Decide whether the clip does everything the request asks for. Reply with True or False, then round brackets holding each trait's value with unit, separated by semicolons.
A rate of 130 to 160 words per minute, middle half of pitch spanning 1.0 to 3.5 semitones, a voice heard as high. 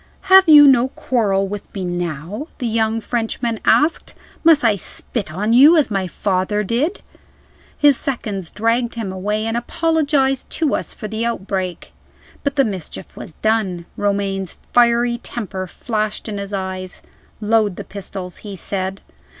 False (150 wpm; 4.0 semitones; 215 Hz)